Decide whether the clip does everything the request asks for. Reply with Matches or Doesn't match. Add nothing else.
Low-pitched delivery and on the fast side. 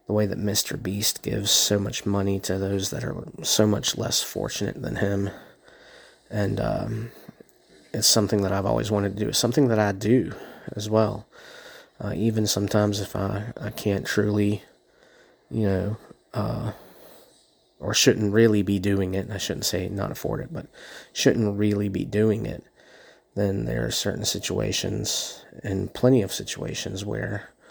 Doesn't match